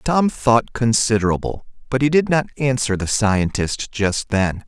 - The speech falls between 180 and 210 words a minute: No, average, 155 wpm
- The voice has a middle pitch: No, low, 115 Hz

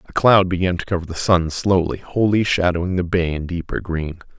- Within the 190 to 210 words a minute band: Yes, fast, 205 wpm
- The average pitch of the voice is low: Yes, very low, 90 Hz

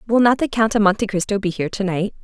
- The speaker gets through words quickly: Yes, fast, 295 wpm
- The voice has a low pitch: No, high, 205 Hz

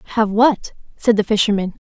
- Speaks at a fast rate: No, average, 160 wpm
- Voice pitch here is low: No, high, 215 Hz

